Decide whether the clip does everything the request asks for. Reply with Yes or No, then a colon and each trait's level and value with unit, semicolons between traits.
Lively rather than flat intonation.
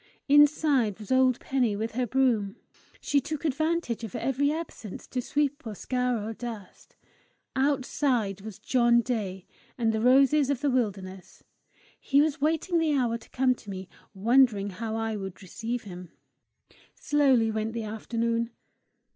No: average, 4.0 semitones